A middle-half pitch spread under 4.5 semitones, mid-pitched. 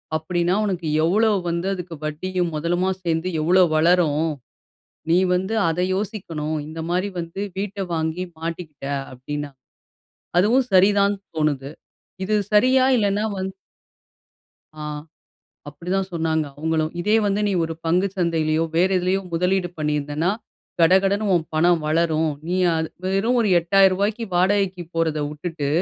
Yes: average, 3.2 semitones; medium, 175 Hz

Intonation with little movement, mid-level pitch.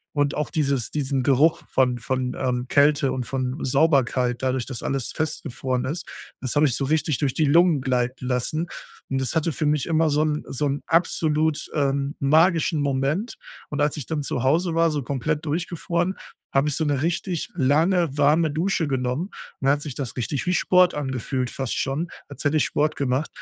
No: average, 3.1 semitones; medium, 145 Hz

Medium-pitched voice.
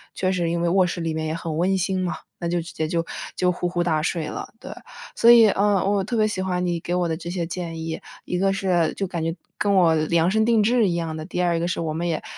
Yes: medium, 175 Hz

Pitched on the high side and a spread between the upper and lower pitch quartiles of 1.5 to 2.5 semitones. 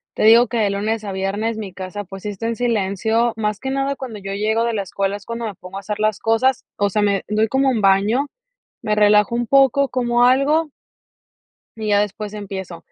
No: high, 215 Hz; average, 2.9 semitones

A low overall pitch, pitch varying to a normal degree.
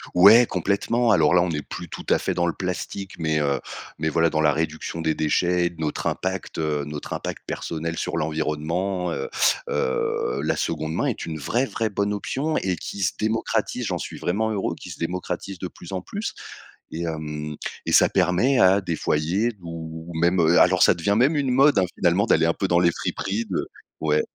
Yes: very low, 85 Hz; average, 3.9 semitones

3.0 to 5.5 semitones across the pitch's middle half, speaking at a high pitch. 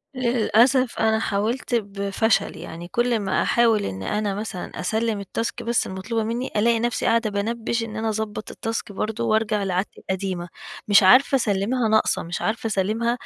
No: narrow, 2.6 semitones; high, 220 Hz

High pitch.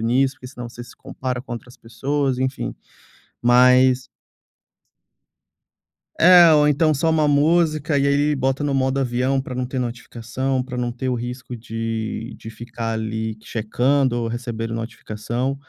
No: low, 125 Hz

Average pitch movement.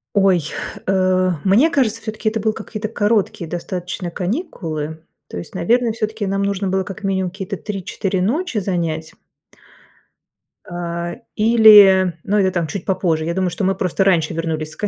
Yes: average, 3.4 semitones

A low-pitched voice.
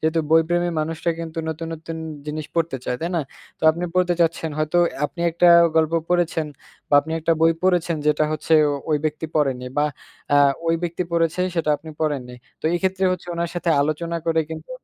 No: medium, 165 Hz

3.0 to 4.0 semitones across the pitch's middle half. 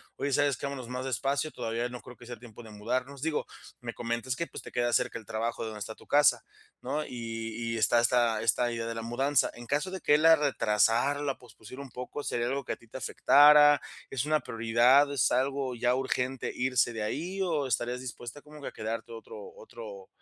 Yes: average, 3.4 semitones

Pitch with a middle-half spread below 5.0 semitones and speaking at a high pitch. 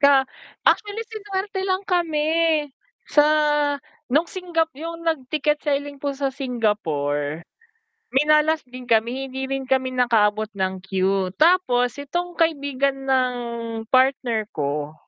No: wide, 5.4 semitones; very high, 270 Hz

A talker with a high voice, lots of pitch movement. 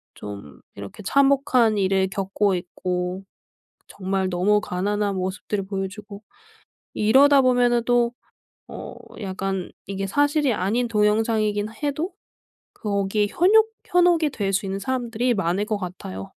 No: high, 205 Hz; average, 4.2 semitones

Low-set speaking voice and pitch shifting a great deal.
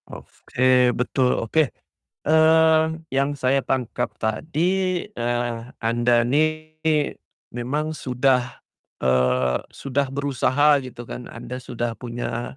No: low, 130 Hz; average, 4.2 semitones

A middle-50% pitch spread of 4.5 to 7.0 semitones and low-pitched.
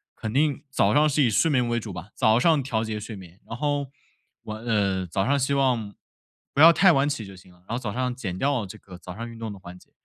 Yes: wide, 5.5 semitones; low, 115 Hz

